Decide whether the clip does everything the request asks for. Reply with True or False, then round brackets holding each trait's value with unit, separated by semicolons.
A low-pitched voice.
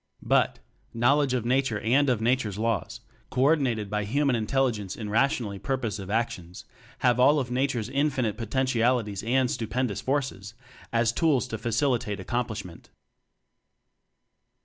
True (120 Hz)